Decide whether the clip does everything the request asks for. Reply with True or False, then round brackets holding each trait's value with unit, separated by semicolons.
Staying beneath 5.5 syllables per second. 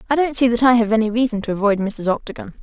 False (7.0 syllables/s)